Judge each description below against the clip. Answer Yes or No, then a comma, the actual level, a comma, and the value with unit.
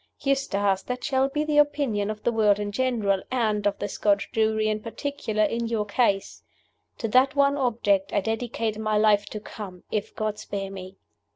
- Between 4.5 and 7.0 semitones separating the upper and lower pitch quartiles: No, average, 3.5 semitones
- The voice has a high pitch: Yes, high, 215 Hz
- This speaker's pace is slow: No, average, 185 wpm